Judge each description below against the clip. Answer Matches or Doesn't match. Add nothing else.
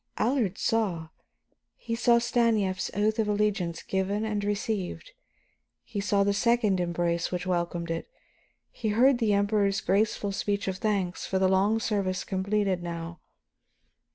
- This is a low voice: Doesn't match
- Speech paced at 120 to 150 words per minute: Matches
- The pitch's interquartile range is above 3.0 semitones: Doesn't match